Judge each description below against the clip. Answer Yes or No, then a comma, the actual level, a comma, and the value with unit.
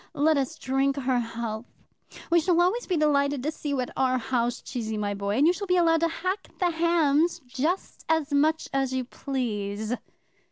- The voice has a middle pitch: No, very high, 280 Hz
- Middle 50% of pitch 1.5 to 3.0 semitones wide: No, average, 4.9 semitones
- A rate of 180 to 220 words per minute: Yes, average, 195 wpm